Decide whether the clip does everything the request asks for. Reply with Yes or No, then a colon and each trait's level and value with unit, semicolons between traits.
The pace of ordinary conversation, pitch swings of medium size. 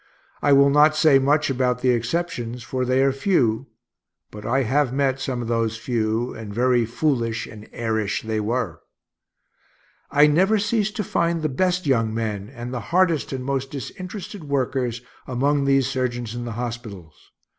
Yes: average, 165 wpm; average, 3.9 semitones